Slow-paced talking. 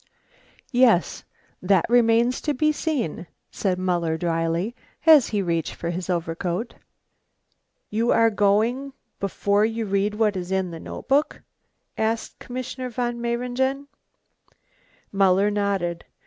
Yes: slow, 120 wpm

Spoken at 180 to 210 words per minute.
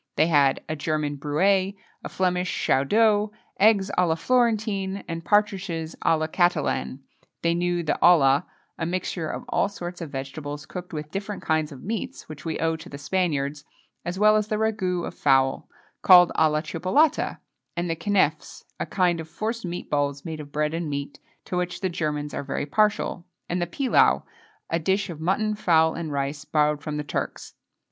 Yes: average, 185 wpm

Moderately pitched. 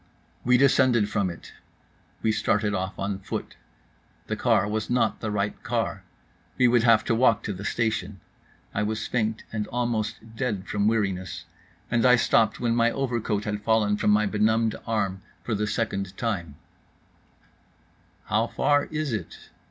No: low, 110 Hz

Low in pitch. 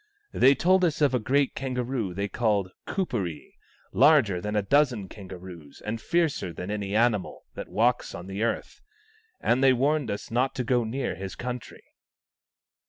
Yes: low, 120 Hz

